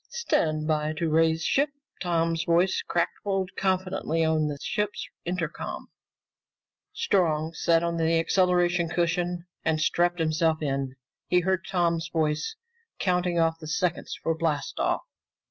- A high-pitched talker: No, medium, 170 Hz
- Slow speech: Yes, slow, 130 wpm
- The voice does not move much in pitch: Yes, narrow, 2.0 semitones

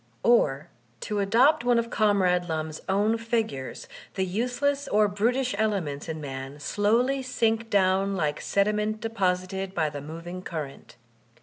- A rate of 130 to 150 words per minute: Yes, slow, 135 wpm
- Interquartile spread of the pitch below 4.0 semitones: No, average, 5.3 semitones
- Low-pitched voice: No, high, 200 Hz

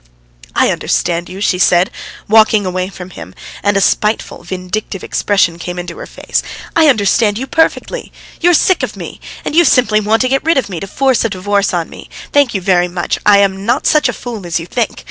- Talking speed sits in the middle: No, fast, 220 wpm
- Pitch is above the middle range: Yes, high, 200 Hz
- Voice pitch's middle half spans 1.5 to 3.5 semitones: No, average, 4.8 semitones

